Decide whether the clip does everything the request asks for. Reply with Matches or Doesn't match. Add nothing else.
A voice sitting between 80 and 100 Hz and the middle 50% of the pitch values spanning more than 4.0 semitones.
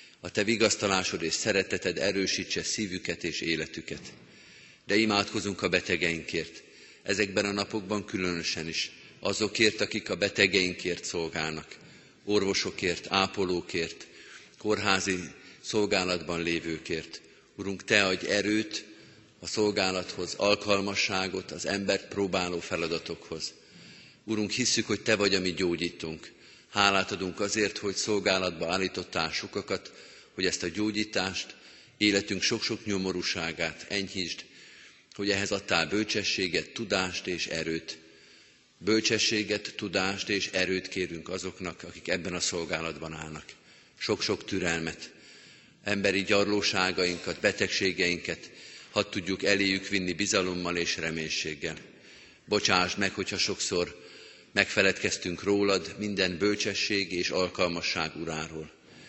Doesn't match